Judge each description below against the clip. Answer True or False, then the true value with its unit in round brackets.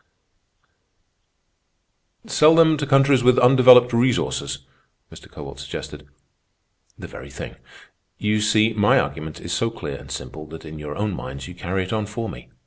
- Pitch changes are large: True (7.5 semitones)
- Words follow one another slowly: False (160 wpm)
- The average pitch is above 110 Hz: False (105 Hz)